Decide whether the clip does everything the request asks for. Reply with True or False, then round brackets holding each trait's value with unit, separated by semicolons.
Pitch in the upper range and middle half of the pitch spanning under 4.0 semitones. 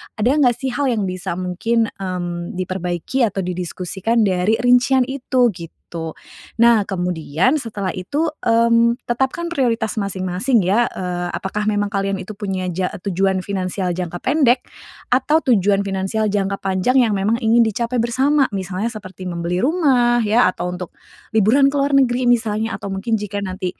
False (210 Hz; 4.6 semitones)